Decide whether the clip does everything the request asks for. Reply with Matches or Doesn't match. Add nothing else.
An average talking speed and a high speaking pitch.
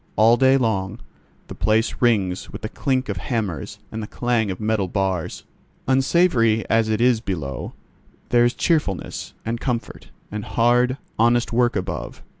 Doesn't match